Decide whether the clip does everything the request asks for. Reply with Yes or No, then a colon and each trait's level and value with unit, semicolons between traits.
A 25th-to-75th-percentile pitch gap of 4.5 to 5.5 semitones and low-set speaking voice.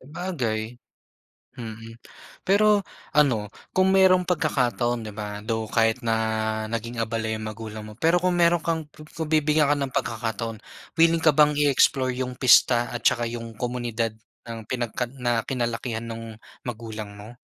Yes: average, 4.9 semitones; low, 120 Hz